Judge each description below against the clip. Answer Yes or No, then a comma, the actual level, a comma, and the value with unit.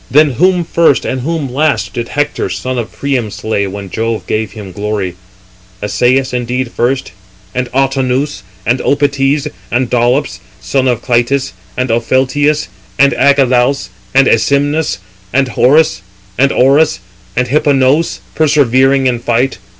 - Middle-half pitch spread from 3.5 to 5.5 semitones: No, average, 3.0 semitones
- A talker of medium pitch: No, low, 130 Hz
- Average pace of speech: No, slow, 125 wpm